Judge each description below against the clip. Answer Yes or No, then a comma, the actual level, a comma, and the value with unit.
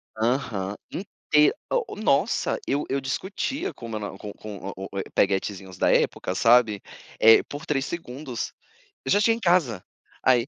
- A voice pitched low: Yes, low, 125 Hz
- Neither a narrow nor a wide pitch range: No, wide, 6.4 semitones